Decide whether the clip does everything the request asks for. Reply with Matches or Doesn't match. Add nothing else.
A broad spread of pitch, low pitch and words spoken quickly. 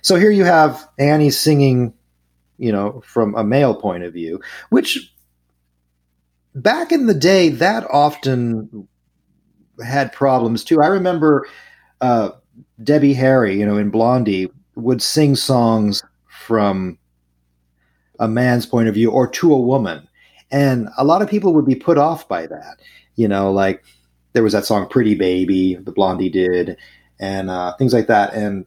Doesn't match